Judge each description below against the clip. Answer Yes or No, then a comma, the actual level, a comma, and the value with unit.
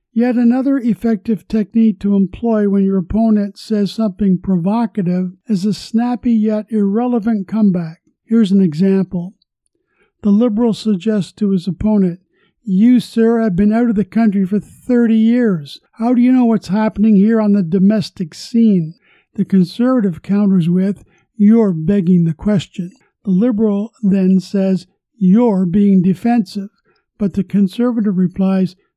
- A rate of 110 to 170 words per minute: Yes, average, 140 wpm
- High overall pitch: Yes, high, 205 Hz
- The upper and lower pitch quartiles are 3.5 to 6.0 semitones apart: No, average, 2.9 semitones